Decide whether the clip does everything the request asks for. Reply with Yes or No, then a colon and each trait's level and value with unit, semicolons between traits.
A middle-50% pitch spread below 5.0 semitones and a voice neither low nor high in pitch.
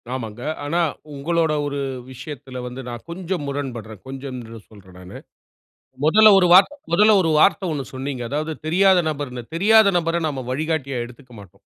No: average, 5.3 semitones; medium, 145 Hz